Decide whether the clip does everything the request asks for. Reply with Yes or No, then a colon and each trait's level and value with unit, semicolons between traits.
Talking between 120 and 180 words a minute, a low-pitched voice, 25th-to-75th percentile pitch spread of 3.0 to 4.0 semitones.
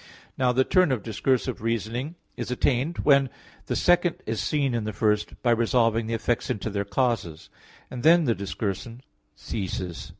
Yes: average, 165 wpm; low, 115 Hz; average, 3.6 semitones